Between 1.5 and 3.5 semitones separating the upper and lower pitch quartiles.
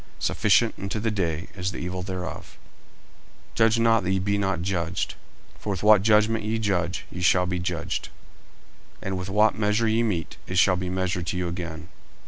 Yes: average, 3.0 semitones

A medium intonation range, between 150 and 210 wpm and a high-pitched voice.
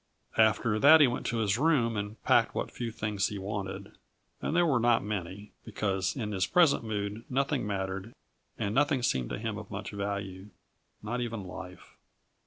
No: average, 3.3 semitones; average, 180 wpm; low, 105 Hz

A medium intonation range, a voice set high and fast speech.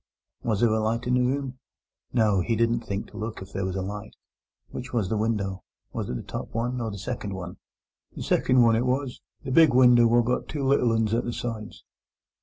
No: average, 3.0 semitones; low, 115 Hz; fast, 220 wpm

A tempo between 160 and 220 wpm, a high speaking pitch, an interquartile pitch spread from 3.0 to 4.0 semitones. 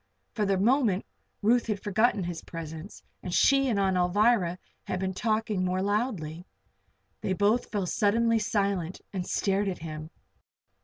No: average, 150 wpm; high, 200 Hz; average, 3.3 semitones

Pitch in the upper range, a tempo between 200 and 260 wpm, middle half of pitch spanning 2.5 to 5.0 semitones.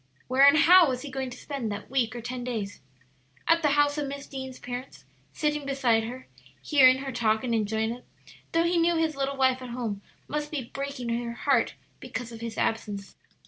Yes: very high, 255 Hz; fast, 205 wpm; average, 3.4 semitones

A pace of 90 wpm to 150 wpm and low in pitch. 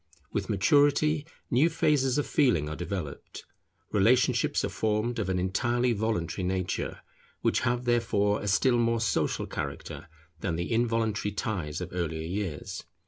Yes: average, 140 wpm; low, 110 Hz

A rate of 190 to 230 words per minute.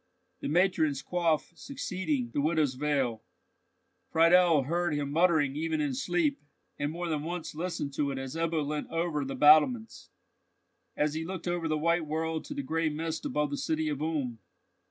No: average, 170 wpm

